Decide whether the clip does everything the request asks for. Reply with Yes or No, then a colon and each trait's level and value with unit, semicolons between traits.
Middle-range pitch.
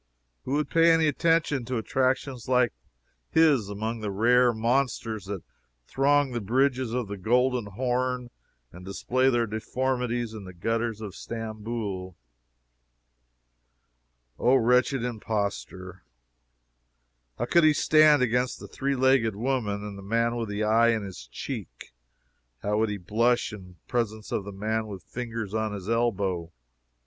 No: low, 115 Hz